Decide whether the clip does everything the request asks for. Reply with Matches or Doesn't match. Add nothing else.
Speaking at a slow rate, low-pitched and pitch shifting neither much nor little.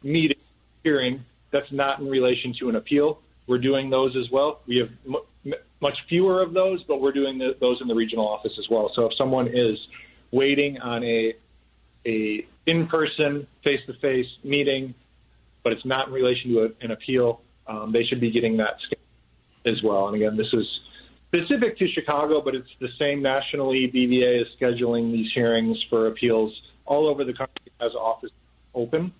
Doesn't match